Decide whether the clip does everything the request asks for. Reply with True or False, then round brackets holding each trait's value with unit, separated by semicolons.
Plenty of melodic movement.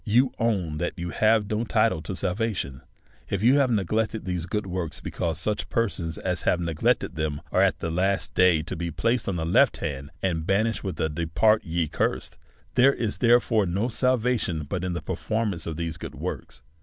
False (5.0 semitones)